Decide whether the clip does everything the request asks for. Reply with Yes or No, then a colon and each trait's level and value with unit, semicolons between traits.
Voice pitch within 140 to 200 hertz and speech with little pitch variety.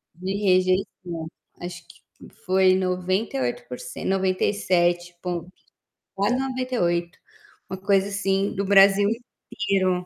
Yes: medium, 185 Hz; narrow, 2.0 semitones